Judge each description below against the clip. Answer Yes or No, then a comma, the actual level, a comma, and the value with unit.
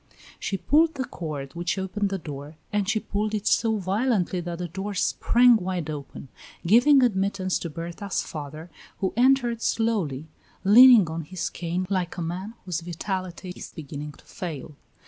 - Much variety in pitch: No, average, 4.3 semitones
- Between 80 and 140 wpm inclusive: No, average, 165 wpm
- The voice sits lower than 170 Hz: No, medium, 185 Hz